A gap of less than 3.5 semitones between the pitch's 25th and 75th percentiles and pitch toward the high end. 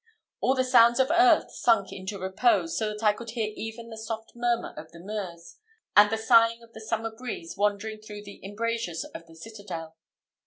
Yes: narrow, 2.4 semitones; high, 220 Hz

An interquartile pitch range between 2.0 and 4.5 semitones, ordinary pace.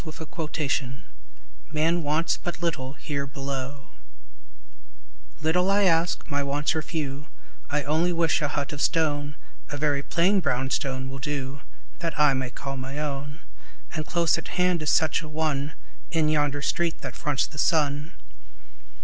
Yes: average, 2.7 semitones; average, 155 wpm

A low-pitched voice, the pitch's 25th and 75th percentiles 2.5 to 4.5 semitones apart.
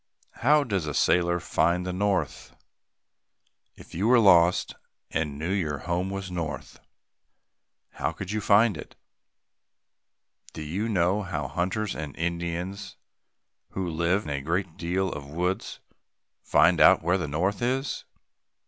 Yes: very low, 90 Hz; average, 3.1 semitones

